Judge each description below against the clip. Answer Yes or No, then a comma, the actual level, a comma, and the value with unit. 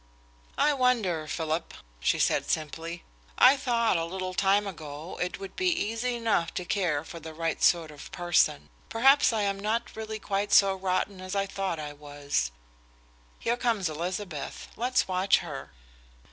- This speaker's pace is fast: No, average, 160 wpm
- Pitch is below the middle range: No, medium, 185 Hz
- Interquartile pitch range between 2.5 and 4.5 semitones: No, average, 5.2 semitones